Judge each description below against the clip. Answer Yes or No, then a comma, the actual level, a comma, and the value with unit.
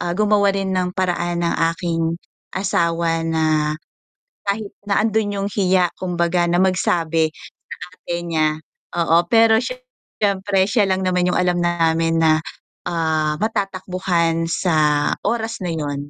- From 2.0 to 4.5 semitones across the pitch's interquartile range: Yes, average, 2.9 semitones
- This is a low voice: No, medium, 175 Hz